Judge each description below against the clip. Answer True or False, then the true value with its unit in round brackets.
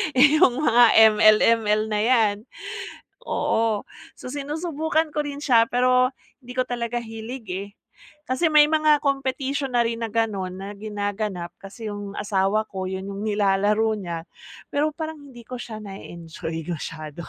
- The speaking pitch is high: True (225 Hz)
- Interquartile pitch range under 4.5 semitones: False (4.9 semitones)